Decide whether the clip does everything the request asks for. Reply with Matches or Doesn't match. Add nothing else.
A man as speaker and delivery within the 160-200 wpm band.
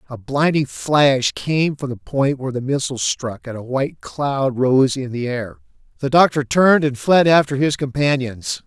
Matches